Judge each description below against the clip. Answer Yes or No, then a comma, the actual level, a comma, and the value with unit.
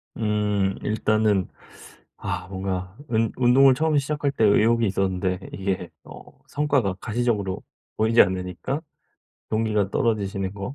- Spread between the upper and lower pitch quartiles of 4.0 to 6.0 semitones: No, average, 3.6 semitones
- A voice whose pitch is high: No, low, 105 Hz